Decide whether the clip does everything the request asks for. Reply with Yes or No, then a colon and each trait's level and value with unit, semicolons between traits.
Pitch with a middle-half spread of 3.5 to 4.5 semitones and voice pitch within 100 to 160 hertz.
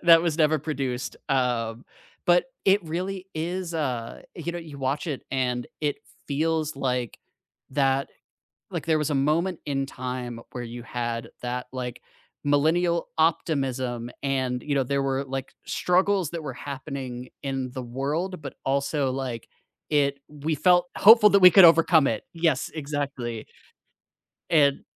Yes: average, 4.2 semitones; medium, 140 Hz